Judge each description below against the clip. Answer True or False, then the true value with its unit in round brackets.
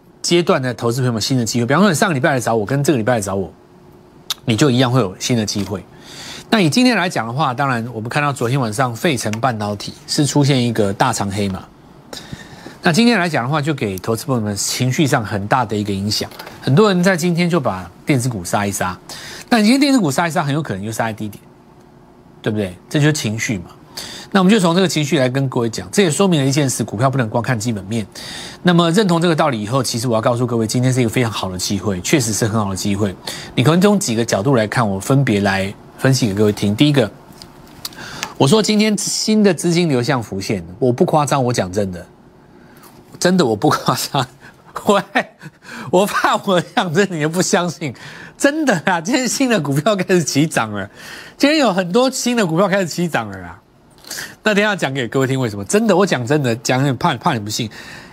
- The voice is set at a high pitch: False (135 Hz)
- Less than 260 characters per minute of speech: False (330 characters per minute)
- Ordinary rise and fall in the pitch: False (7.7 semitones)